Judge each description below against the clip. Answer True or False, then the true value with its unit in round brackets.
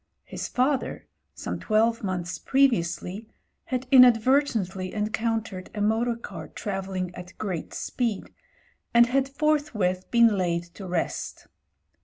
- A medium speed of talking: False (120 wpm)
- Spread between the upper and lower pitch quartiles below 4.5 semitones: False (4.8 semitones)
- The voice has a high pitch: True (220 Hz)